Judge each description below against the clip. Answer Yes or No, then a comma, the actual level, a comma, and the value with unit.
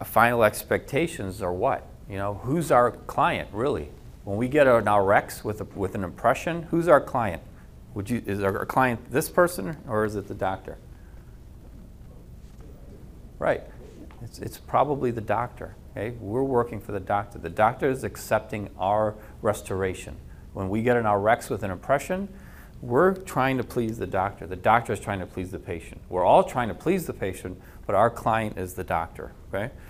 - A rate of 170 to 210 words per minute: Yes, average, 180 wpm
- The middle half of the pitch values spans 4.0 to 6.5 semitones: Yes, average, 4.5 semitones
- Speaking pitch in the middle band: No, low, 105 Hz